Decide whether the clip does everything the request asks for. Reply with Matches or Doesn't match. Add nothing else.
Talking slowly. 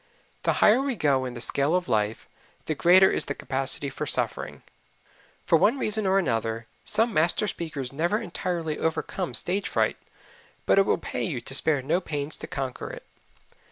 Doesn't match